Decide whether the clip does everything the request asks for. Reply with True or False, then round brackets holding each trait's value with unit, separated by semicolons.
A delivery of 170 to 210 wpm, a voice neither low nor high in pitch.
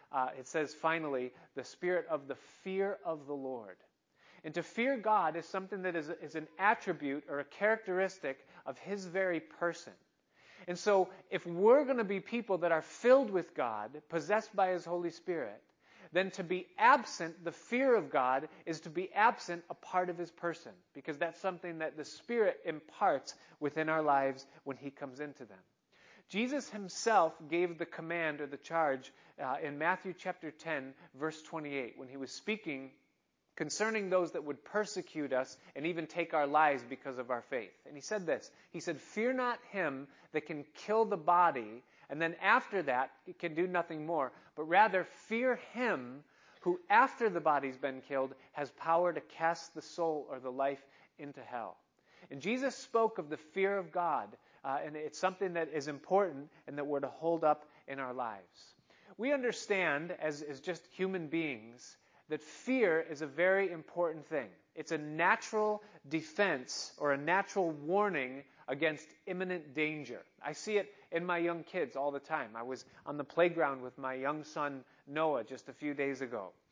True (180 wpm; 165 Hz)